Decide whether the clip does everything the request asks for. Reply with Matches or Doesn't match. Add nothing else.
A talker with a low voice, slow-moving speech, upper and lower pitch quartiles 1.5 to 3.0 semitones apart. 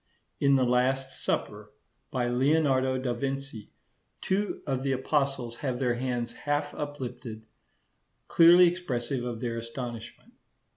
Matches